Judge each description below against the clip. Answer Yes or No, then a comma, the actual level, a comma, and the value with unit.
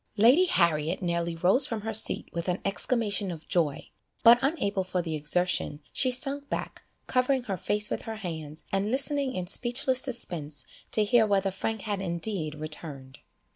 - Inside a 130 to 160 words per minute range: No, average, 170 wpm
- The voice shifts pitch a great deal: Yes, wide, 6.0 semitones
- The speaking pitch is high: Yes, high, 195 Hz